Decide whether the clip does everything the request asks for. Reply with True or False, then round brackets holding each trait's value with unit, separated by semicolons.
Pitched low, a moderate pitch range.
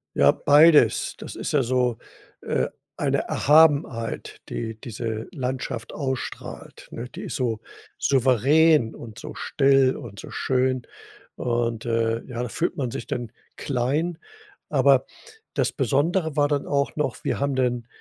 True (130 Hz; 3.6 semitones)